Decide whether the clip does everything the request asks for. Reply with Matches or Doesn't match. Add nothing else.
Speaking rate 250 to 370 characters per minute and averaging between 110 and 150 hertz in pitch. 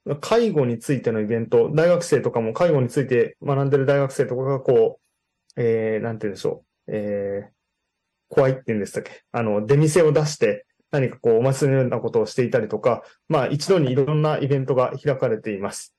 Doesn't match